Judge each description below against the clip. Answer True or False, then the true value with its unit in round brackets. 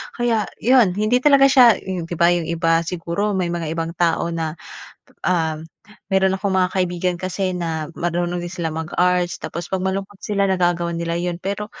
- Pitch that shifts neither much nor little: False (2.2 semitones)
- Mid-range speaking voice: True (180 Hz)